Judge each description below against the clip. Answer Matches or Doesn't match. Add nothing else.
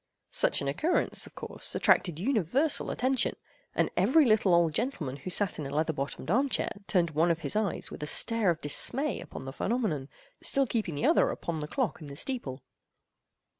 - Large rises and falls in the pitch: Matches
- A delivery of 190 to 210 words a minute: Matches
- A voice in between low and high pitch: Matches